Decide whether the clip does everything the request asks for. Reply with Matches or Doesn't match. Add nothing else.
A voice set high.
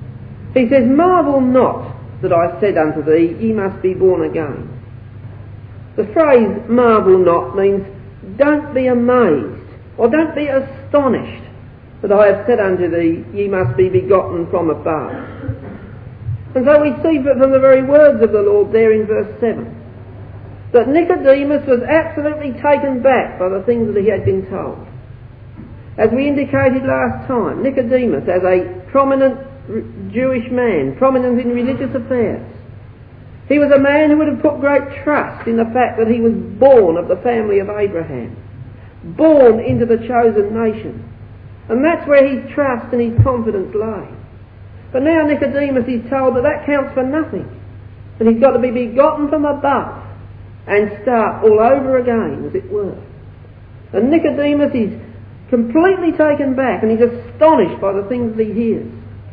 Matches